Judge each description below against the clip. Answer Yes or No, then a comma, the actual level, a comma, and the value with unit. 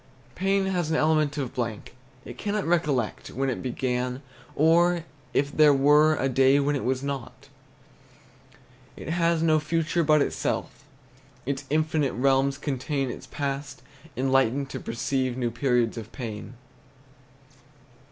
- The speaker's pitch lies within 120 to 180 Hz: Yes, medium, 140 Hz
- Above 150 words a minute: No, slow, 135 wpm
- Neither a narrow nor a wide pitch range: Yes, average, 3.2 semitones